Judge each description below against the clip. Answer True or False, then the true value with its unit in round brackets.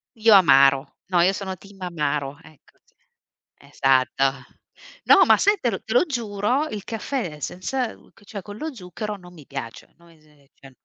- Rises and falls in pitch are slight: False (7.1 semitones)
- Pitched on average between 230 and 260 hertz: False (185 Hz)